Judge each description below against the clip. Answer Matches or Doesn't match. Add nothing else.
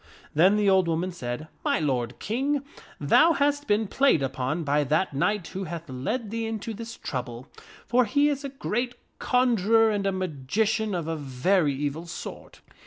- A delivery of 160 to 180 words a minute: Matches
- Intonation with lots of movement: Matches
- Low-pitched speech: Doesn't match